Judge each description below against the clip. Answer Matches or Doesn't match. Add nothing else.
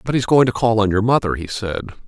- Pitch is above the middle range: Doesn't match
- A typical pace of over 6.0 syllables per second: Matches